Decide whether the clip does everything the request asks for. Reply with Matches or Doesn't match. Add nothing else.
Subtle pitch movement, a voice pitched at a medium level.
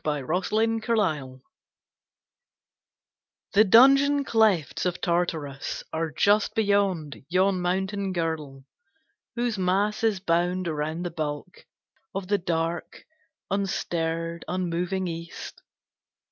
Doesn't match